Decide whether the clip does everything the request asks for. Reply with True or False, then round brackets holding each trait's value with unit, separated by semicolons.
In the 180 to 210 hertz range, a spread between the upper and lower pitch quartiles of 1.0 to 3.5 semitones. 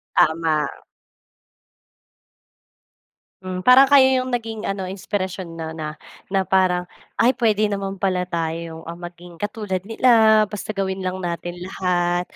True (185 Hz; 3.2 semitones)